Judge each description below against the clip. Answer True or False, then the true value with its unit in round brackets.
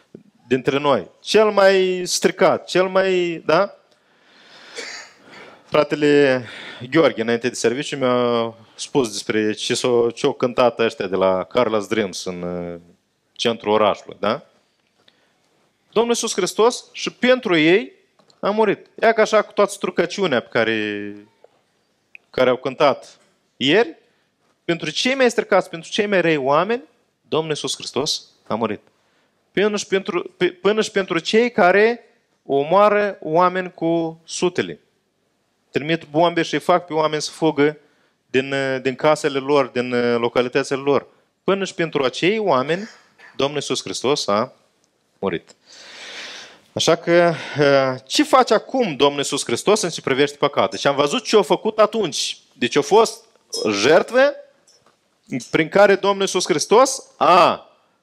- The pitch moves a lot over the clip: True (7.1 semitones)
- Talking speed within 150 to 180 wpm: False (130 wpm)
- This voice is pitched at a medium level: True (160 Hz)